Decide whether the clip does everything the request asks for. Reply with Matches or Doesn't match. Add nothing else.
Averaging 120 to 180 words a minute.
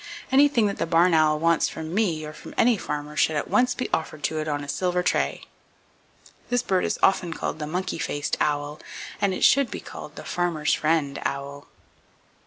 Doesn't match